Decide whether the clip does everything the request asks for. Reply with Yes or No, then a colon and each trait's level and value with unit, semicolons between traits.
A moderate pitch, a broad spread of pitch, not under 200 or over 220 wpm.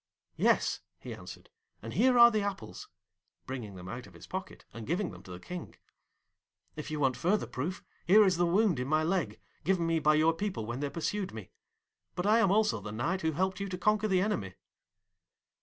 Yes: medium, 170 Hz; wide, 6.8 semitones; fast, 205 wpm